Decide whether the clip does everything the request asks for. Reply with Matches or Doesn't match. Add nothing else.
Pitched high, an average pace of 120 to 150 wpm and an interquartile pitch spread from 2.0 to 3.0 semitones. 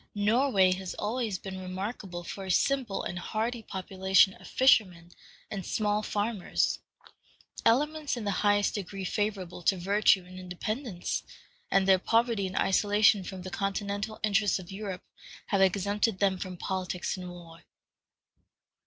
Matches